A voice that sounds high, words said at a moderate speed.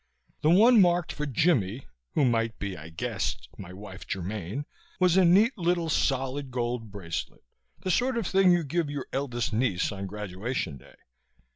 No: low, 130 Hz; average, 165 wpm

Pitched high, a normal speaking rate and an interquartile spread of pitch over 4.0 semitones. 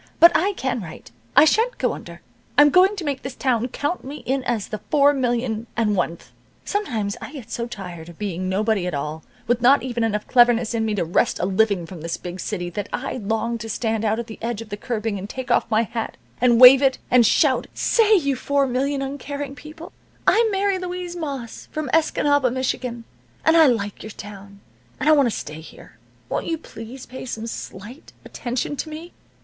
No: high, 240 Hz; fast, 210 wpm; average, 5.1 semitones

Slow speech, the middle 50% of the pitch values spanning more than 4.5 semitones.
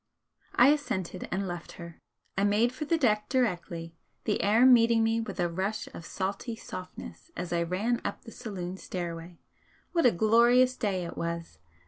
No: average, 170 wpm; average, 5.2 semitones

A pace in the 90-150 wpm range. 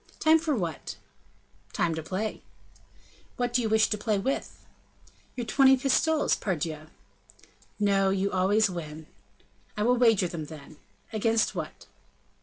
Yes: slow, 135 wpm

